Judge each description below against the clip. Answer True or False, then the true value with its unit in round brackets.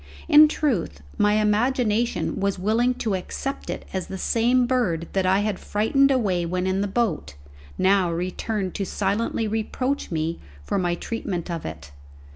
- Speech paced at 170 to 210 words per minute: False (160 wpm)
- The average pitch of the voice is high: True (200 Hz)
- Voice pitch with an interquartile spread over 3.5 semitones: True (4.4 semitones)